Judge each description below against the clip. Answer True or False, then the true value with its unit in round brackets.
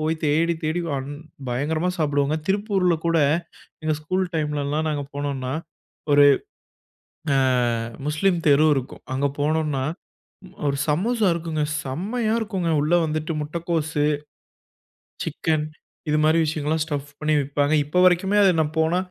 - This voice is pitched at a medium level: True (155 Hz)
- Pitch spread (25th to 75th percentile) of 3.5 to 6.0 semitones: False (2.8 semitones)